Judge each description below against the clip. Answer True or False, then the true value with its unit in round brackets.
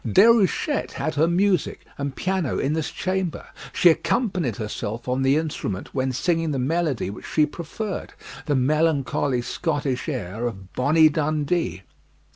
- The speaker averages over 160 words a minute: False (140 wpm)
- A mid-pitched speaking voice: True (150 Hz)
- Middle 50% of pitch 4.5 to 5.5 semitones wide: True (4.9 semitones)